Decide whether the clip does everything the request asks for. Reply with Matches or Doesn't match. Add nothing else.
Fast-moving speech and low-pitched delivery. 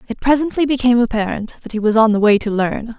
Doesn't match